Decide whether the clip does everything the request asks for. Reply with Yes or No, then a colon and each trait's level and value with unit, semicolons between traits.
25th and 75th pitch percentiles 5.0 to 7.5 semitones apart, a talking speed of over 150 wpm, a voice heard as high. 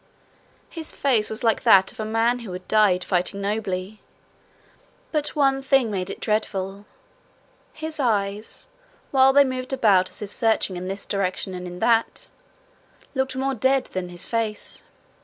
Yes: average, 5.3 semitones; average, 160 wpm; high, 215 Hz